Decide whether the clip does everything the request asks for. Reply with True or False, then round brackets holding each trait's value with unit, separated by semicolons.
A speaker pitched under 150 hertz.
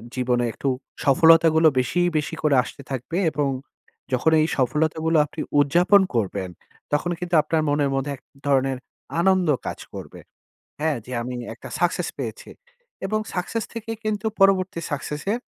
False (155 Hz)